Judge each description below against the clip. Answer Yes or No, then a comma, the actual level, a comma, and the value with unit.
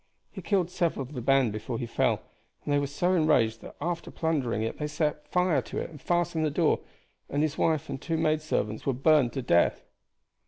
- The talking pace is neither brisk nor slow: No, fast, 220 wpm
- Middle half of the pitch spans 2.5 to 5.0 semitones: Yes, average, 4.2 semitones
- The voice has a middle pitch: Yes, medium, 150 Hz